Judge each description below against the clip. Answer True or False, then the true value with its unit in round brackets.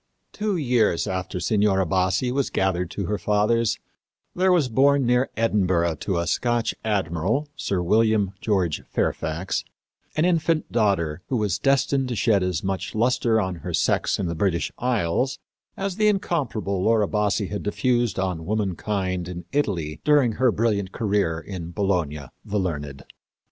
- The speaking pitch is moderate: False (105 Hz)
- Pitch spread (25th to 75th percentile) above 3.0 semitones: True (5.2 semitones)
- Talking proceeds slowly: False (155 wpm)